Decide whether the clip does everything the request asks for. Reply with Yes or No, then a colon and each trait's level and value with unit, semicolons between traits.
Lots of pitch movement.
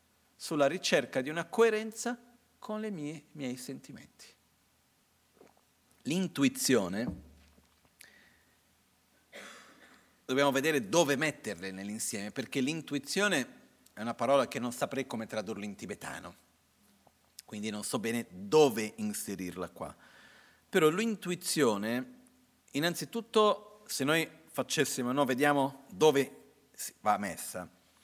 Yes: wide, 8.7 semitones